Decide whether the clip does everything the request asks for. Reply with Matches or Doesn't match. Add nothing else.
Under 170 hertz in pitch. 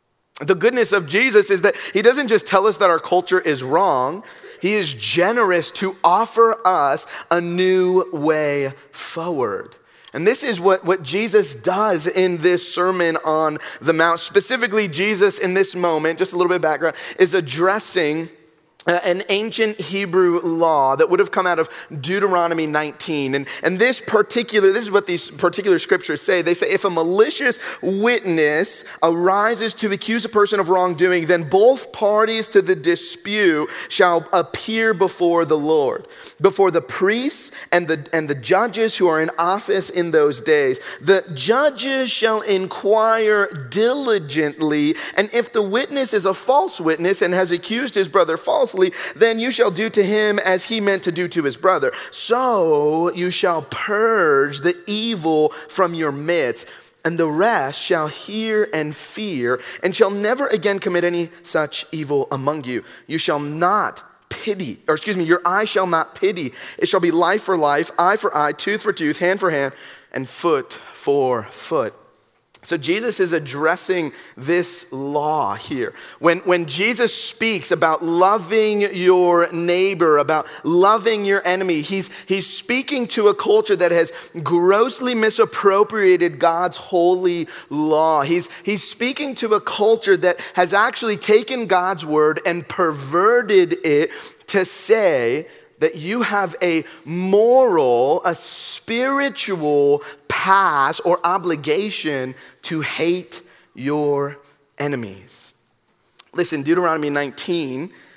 Doesn't match